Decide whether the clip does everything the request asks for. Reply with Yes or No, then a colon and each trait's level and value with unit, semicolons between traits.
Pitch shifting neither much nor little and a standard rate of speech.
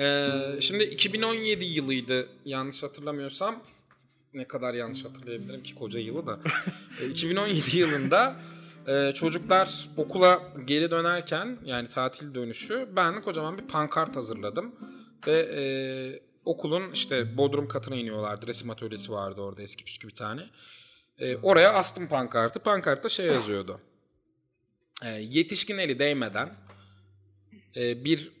No: wide, 6.5 semitones; average, 125 wpm